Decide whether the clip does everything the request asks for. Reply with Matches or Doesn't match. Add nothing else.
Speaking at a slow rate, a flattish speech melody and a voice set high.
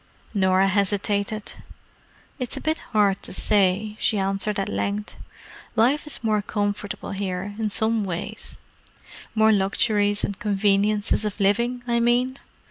Matches